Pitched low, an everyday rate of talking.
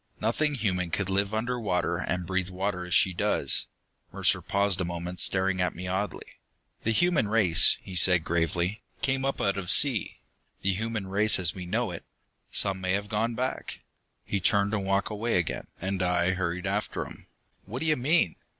Yes: very low, 95 Hz; average, 185 wpm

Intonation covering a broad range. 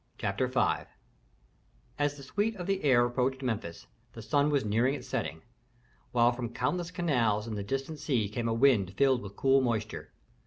No: average, 4.2 semitones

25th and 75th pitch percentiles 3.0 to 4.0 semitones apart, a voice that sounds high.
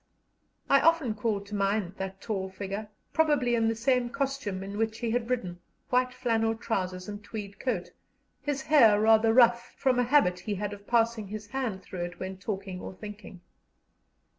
Yes: average, 3.6 semitones; high, 220 Hz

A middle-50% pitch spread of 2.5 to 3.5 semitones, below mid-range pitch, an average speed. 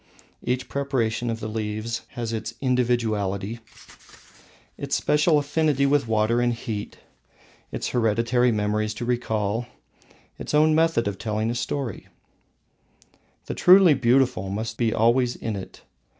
No: average, 3.0 semitones; low, 115 Hz; slow, 110 wpm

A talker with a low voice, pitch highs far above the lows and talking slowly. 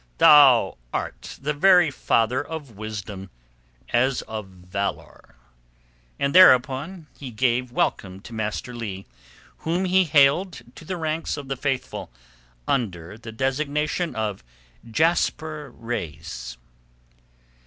Yes: low, 130 Hz; wide, 6.1 semitones; slow, 110 wpm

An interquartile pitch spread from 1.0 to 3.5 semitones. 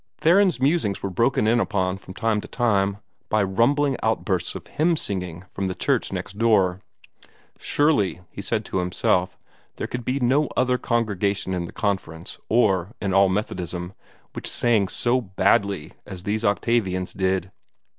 No: average, 4.3 semitones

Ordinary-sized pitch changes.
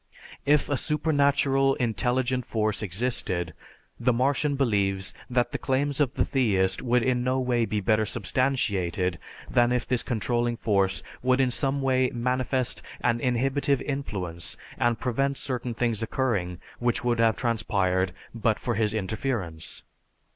Yes: average, 3.5 semitones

